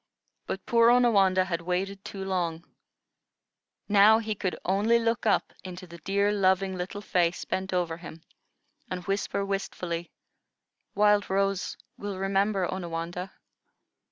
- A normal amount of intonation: No, narrow, 2.2 semitones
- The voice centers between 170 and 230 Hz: Yes, high, 190 Hz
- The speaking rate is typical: No, slow, 125 wpm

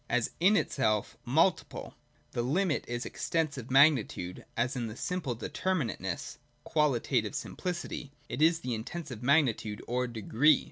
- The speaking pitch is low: Yes, low, 130 Hz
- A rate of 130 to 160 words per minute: Yes, slow, 135 wpm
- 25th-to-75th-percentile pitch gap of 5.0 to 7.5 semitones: Yes, average, 5.3 semitones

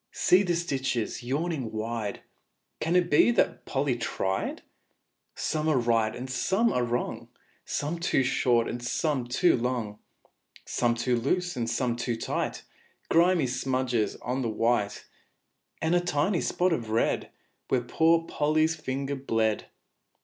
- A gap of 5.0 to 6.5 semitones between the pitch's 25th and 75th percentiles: Yes, average, 5.3 semitones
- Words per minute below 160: Yes, average, 140 wpm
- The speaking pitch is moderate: No, low, 130 Hz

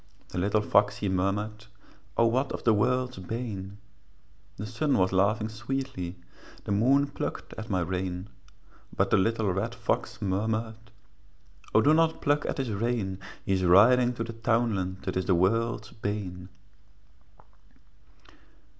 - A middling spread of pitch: Yes, average, 3.6 semitones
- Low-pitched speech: Yes, low, 110 Hz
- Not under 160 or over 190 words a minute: No, average, 145 wpm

